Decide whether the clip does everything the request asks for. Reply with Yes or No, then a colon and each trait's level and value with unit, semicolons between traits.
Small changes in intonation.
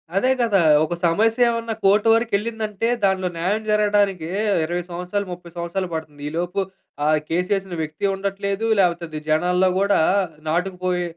No: average, 3.0 semitones